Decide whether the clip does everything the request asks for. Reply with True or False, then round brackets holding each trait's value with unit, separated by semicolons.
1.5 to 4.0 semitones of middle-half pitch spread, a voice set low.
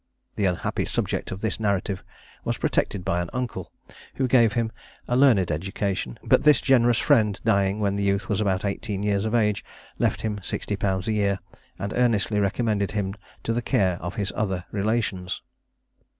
True (2.6 semitones; 100 Hz)